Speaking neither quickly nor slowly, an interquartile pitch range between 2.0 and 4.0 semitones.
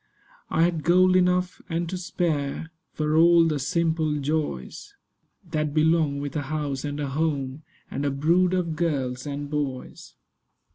Yes: average, 155 wpm; average, 2.9 semitones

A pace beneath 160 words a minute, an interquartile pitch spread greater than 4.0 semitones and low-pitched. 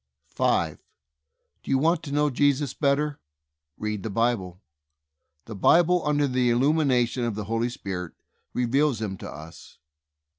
Yes: average, 145 wpm; average, 5.2 semitones; low, 125 Hz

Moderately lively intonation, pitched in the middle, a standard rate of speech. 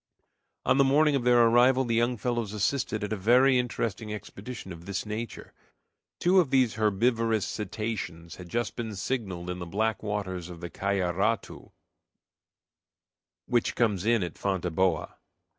No: average, 4.2 semitones; low, 110 Hz; average, 150 wpm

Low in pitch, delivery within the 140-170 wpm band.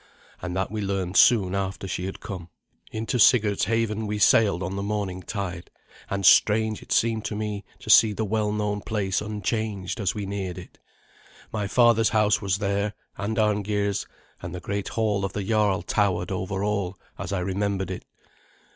No: low, 100 Hz; average, 180 wpm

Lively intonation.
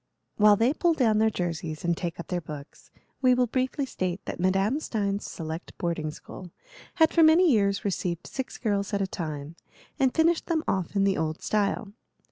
Yes: wide, 6.7 semitones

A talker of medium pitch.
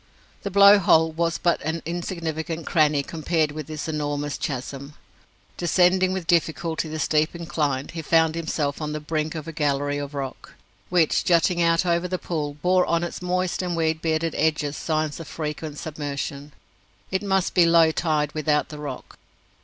Yes: medium, 160 Hz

